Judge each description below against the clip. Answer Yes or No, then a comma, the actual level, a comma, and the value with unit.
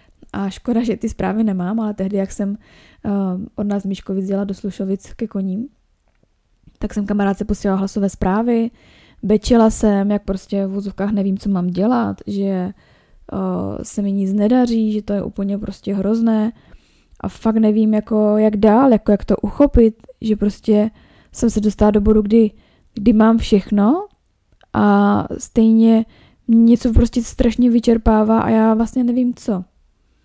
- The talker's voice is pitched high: Yes, high, 210 Hz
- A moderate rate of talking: Yes, average, 155 wpm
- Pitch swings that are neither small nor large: No, narrow, 2.3 semitones